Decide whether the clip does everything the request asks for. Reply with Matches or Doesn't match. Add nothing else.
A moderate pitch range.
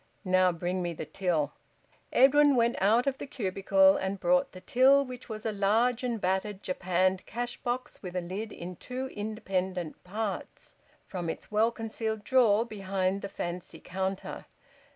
Matches